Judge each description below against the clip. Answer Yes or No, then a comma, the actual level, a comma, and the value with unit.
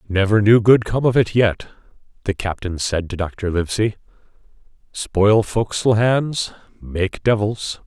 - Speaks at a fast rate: No, slow, 135 wpm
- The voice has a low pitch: Yes, low, 105 Hz